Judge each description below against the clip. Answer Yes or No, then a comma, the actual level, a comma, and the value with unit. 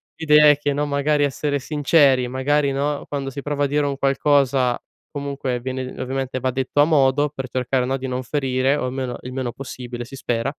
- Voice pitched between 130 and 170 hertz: Yes, low, 135 Hz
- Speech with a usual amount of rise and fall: No, narrow, 2.0 semitones